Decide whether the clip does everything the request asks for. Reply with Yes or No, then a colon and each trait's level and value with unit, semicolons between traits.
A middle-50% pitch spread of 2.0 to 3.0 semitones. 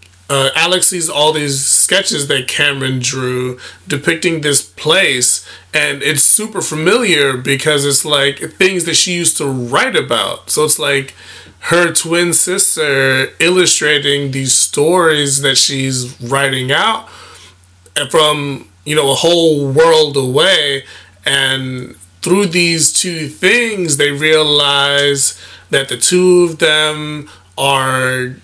No: average, 3.8 semitones